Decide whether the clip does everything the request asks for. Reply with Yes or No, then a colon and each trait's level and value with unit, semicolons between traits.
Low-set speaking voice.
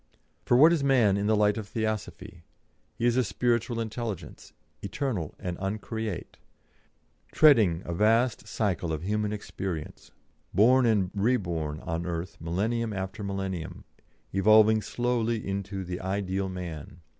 Yes: low, 105 Hz